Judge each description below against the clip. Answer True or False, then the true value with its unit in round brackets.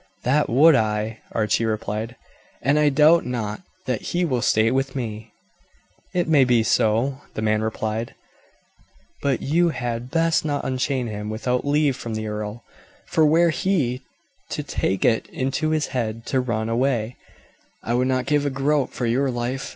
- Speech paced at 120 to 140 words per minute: False (165 wpm)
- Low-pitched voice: True (125 Hz)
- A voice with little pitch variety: False (4.2 semitones)